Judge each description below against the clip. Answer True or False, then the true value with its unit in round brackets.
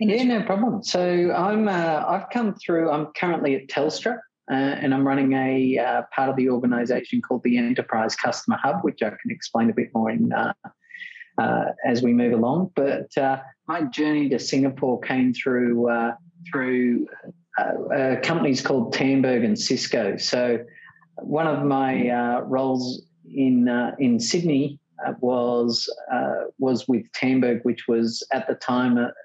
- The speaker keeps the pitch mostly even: False (5.3 semitones)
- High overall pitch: False (135 Hz)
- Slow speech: False (165 wpm)